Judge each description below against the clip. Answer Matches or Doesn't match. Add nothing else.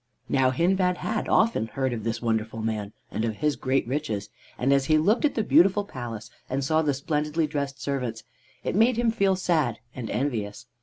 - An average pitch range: Doesn't match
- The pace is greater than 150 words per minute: Matches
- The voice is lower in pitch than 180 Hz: Matches